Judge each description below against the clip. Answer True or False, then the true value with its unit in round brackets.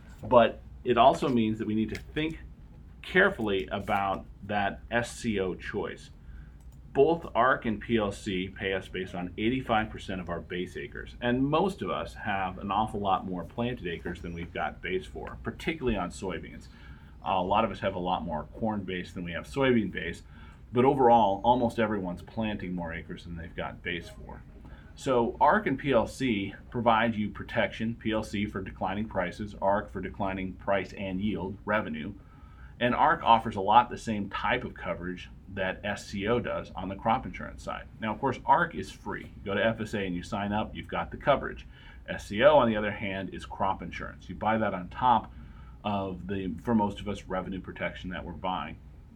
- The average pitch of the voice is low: True (100 Hz)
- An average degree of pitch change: True (3.7 semitones)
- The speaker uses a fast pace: False (185 wpm)